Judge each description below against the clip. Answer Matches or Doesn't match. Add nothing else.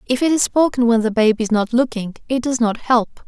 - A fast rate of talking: Matches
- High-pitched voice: Matches